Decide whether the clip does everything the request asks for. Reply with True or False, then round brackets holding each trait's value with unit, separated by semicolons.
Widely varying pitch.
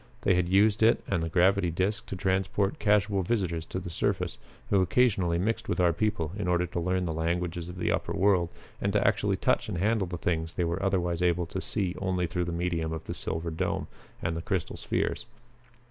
False (2.4 semitones)